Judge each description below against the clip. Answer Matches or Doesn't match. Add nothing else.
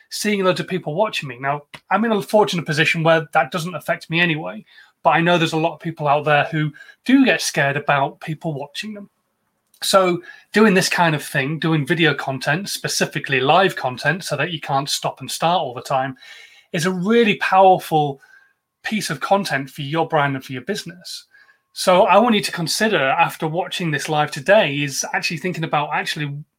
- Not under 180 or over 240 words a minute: Matches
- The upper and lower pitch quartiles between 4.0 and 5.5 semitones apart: Matches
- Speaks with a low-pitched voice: Doesn't match